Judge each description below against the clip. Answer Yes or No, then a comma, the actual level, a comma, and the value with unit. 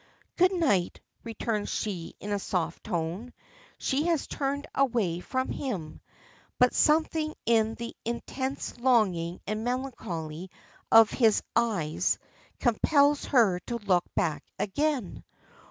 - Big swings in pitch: Yes, wide, 6.3 semitones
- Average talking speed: No, slow, 120 wpm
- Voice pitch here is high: Yes, high, 230 Hz